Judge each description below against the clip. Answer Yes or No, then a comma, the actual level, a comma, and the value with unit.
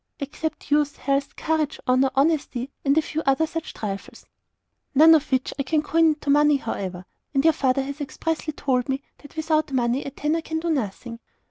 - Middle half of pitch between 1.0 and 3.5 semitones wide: Yes, average, 2.9 semitones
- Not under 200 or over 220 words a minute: No, average, 190 wpm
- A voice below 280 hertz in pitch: No, very high, 285 Hz